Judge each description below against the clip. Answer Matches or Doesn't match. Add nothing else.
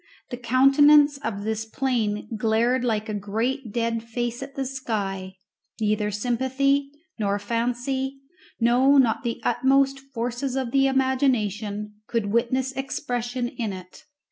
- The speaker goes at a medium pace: Doesn't match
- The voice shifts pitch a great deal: Doesn't match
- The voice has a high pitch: Matches